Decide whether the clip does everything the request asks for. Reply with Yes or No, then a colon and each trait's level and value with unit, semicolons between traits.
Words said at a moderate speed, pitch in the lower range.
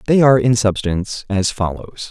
Yes: average, 170 wpm; low, 110 Hz